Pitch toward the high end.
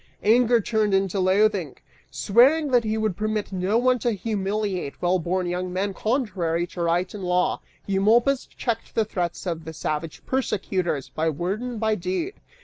Yes: high, 195 Hz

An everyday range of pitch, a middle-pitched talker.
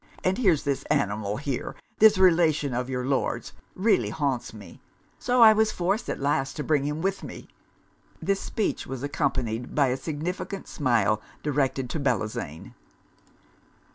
No: wide, 6.3 semitones; medium, 145 Hz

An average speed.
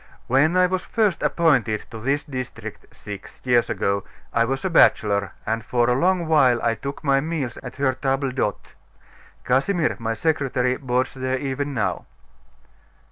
Yes: average, 160 wpm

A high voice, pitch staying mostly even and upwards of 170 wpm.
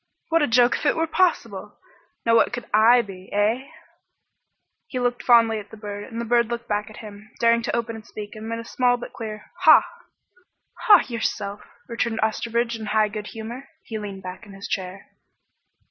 Yes: high, 225 Hz; narrow, 2.2 semitones; average, 195 wpm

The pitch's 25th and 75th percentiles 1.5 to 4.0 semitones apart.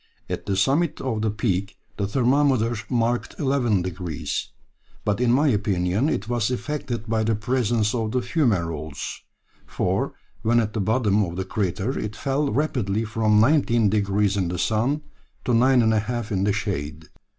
Yes: average, 3.7 semitones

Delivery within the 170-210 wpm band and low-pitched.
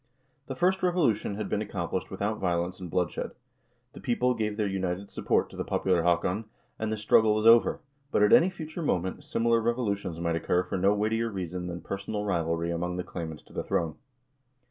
Yes: average, 195 wpm; low, 100 Hz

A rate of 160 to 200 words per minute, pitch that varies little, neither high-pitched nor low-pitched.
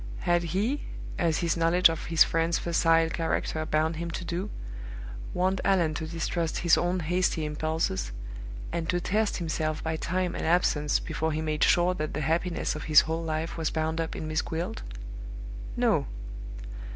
Yes: average, 170 wpm; narrow, 1.8 semitones; medium, 165 Hz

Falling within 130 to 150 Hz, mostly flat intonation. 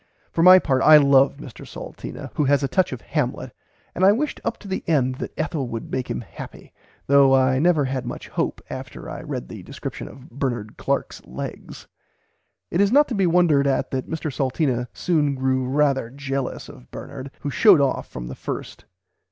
No: medium, 140 Hz; average, 3.8 semitones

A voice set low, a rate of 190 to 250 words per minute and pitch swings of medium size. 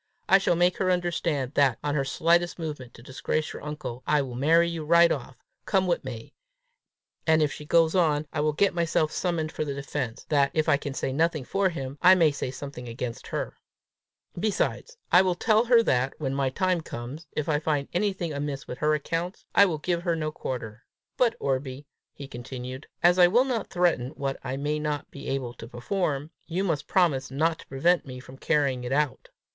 No: medium, 150 Hz; fast, 205 wpm; average, 4.2 semitones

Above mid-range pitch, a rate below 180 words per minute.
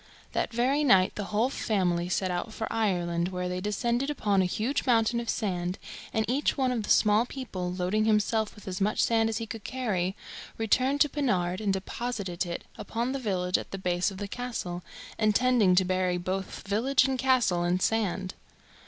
No: high, 210 Hz; average, 190 wpm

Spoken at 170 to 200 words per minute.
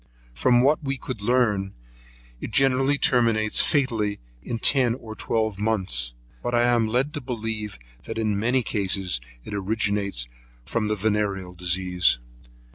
No: average, 140 wpm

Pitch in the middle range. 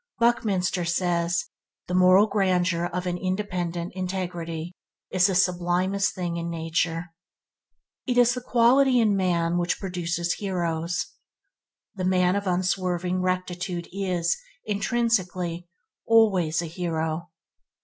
Yes: medium, 180 Hz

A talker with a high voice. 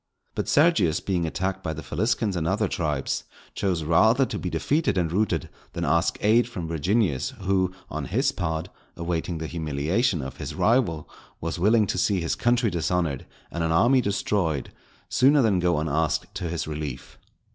No: very low, 90 Hz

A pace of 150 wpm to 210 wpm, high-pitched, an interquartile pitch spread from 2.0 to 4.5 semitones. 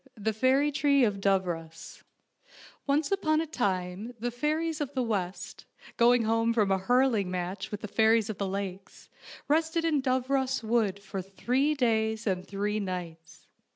No: average, 160 wpm; high, 225 Hz; wide, 5.5 semitones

